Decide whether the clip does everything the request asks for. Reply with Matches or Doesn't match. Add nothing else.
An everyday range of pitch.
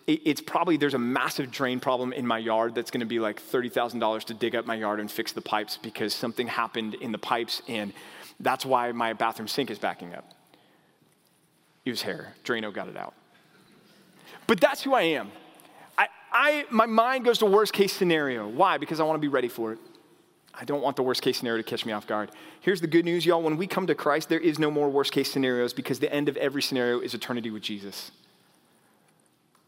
Doesn't match